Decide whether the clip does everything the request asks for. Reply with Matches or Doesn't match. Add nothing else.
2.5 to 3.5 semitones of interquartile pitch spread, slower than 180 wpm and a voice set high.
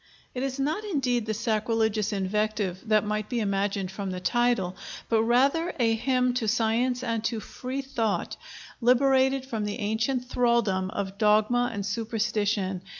Matches